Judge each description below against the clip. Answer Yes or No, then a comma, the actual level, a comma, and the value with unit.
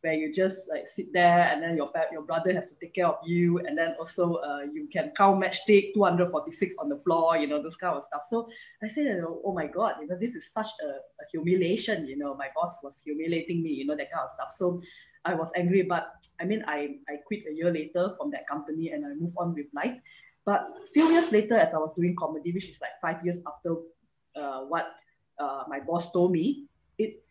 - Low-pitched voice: No, medium, 175 Hz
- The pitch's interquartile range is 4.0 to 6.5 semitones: Yes, average, 5.1 semitones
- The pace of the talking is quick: Yes, fast, 240 wpm